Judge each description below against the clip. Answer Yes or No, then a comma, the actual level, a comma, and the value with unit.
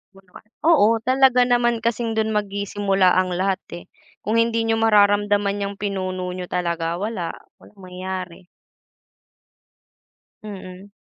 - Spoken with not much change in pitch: No, average, 3.3 semitones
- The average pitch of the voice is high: Yes, high, 200 Hz